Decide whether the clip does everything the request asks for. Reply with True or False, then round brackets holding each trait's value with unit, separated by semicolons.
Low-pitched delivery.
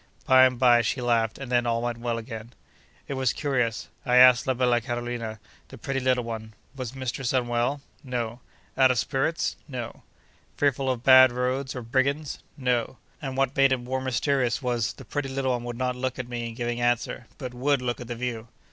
True (125 Hz)